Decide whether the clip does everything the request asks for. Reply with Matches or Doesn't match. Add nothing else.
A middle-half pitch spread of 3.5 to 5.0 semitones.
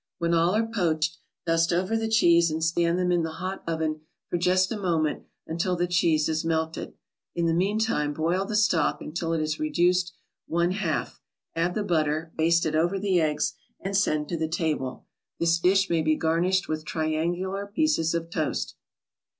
Doesn't match